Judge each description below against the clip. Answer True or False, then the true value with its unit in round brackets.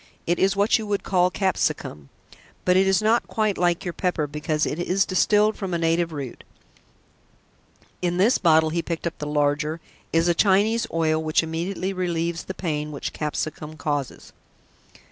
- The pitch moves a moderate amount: True (3.4 semitones)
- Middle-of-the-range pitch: True (170 Hz)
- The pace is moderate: True (170 wpm)